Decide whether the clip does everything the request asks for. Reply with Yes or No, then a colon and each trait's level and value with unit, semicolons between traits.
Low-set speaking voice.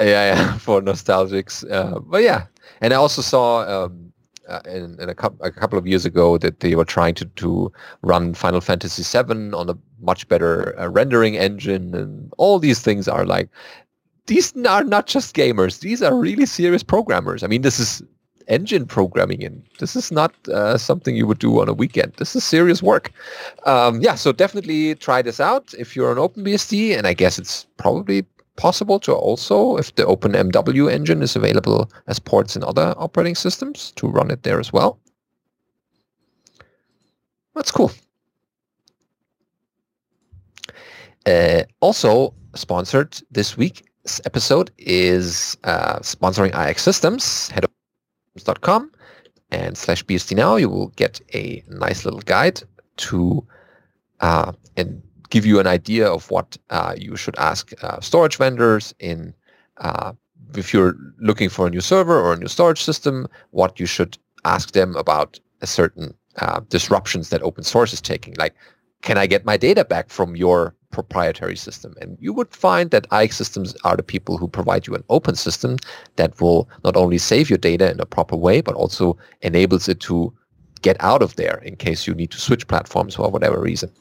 Yes: low, 105 Hz